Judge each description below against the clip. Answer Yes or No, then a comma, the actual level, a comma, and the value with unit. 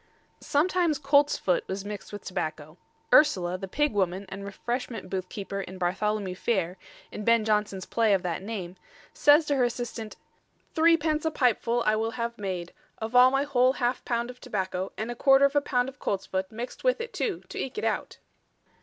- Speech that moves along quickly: No, average, 190 wpm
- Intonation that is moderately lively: No, wide, 5.9 semitones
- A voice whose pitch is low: No, high, 225 Hz